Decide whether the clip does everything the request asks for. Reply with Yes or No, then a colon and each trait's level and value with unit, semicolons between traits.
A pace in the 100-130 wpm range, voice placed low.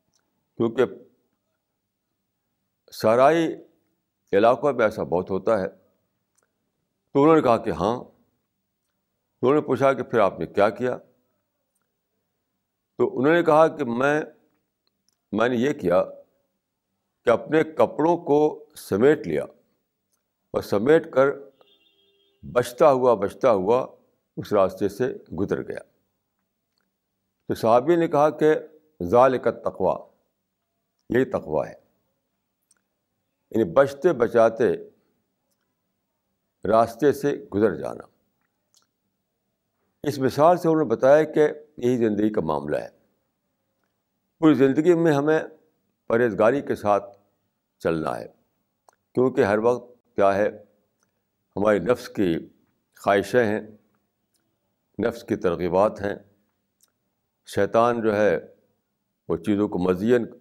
Yes: slow, 110 wpm; low, 125 Hz